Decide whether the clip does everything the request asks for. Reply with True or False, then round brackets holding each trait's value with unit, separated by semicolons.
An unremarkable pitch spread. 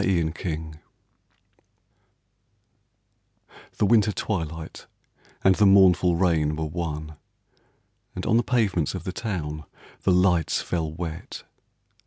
True (3.3 semitones)